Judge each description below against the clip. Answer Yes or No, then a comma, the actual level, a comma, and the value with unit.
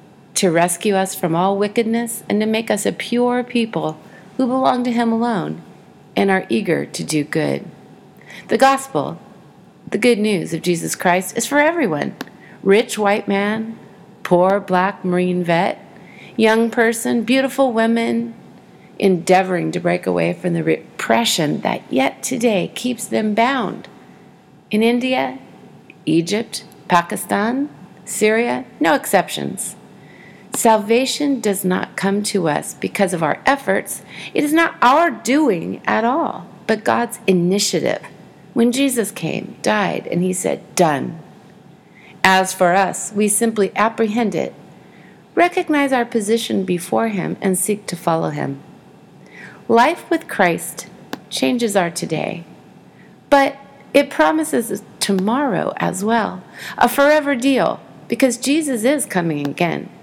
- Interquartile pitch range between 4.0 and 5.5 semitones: Yes, average, 4.3 semitones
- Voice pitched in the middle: No, high, 205 Hz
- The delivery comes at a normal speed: No, slow, 130 wpm